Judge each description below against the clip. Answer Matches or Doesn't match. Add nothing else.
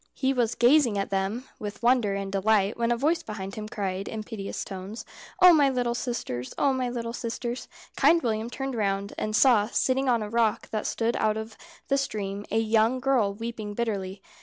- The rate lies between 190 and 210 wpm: Matches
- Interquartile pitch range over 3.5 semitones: Doesn't match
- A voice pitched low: Doesn't match